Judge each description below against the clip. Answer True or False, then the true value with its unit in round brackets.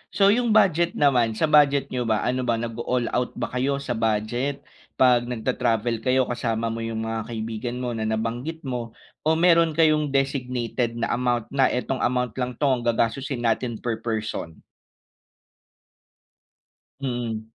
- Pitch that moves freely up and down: False (3.0 semitones)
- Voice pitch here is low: True (125 Hz)